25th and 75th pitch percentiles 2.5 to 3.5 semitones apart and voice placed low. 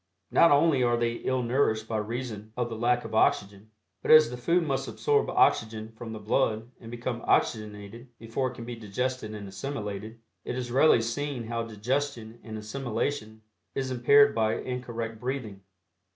Yes: average, 2.9 semitones; low, 115 Hz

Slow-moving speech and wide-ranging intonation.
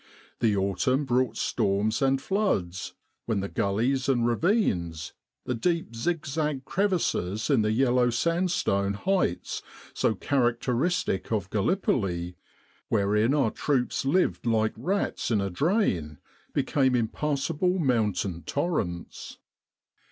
Yes: slow, 115 wpm; wide, 6.9 semitones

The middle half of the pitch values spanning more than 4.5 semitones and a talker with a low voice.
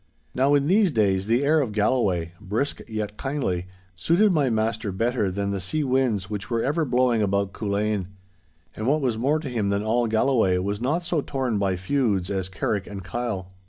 Yes: average, 5.1 semitones; low, 110 Hz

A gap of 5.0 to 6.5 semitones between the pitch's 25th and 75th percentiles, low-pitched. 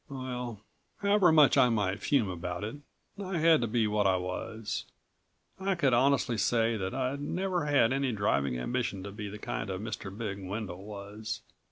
Yes: wide, 5.5 semitones; low, 115 Hz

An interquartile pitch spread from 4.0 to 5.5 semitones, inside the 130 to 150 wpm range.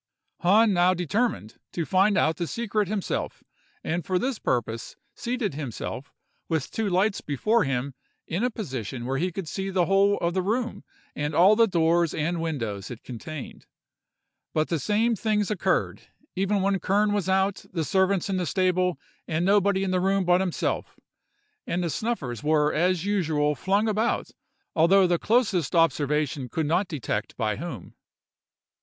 No: average, 4.6 semitones; average, 160 wpm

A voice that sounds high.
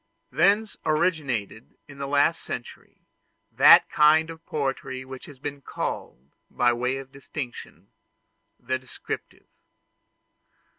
No: medium, 140 Hz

